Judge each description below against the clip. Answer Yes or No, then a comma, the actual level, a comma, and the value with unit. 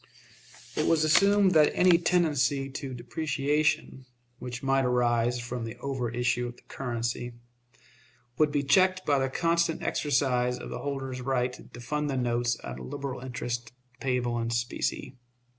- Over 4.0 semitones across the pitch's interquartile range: No, average, 3.4 semitones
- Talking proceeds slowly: No, average, 155 wpm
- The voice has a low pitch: Yes, low, 130 Hz